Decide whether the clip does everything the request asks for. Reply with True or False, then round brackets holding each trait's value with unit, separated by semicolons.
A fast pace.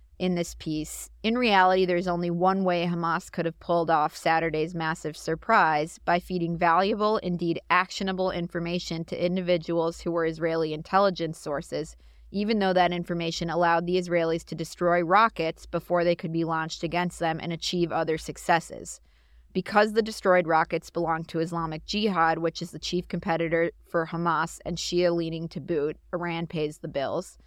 False (165 wpm)